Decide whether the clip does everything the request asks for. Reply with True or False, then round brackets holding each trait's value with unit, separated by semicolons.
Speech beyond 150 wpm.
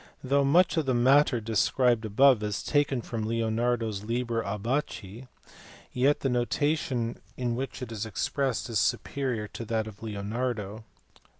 False (145 wpm)